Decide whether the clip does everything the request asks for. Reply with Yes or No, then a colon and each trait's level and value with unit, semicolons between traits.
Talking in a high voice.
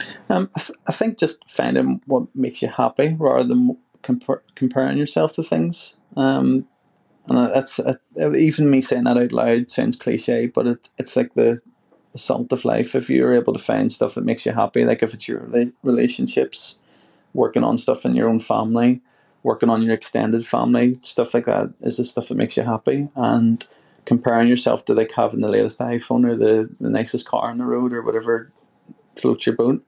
No: low, 120 Hz